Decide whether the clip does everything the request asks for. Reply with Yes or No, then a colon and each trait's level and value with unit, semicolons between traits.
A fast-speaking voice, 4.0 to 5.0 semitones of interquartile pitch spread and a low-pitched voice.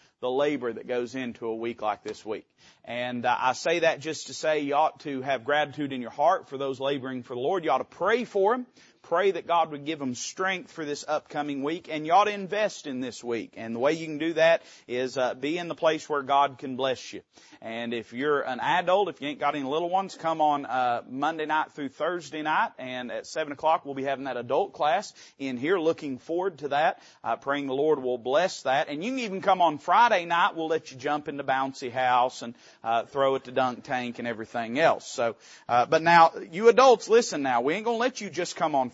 No: fast, 245 wpm; average, 4.3 semitones; medium, 145 Hz